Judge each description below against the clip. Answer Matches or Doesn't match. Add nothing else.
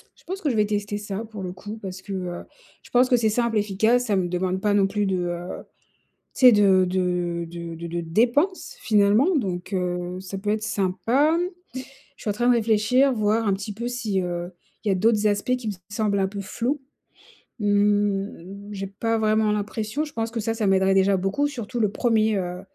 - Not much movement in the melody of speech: Doesn't match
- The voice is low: Doesn't match